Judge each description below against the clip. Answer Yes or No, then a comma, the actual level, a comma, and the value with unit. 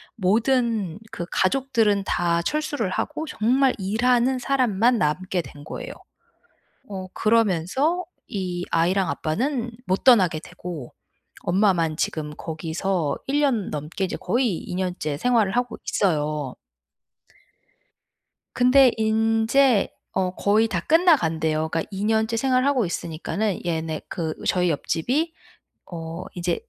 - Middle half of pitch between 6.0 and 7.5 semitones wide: Yes, wide, 6.4 semitones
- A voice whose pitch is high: Yes, high, 195 Hz